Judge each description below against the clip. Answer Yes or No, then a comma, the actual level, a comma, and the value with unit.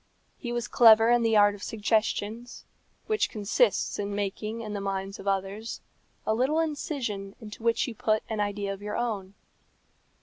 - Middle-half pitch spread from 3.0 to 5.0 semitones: No, narrow, 2.5 semitones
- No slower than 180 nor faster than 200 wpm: No, average, 170 wpm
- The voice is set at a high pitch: Yes, high, 215 Hz